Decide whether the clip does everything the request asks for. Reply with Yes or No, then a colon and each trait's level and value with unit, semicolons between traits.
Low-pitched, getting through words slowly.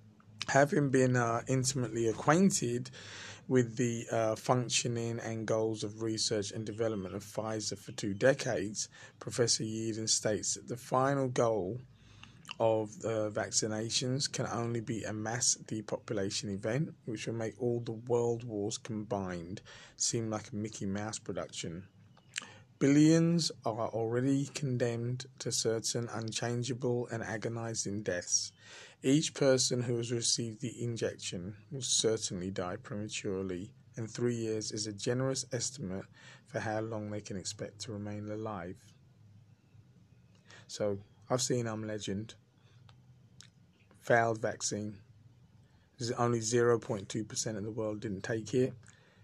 Yes: low, 115 Hz; slow, 130 wpm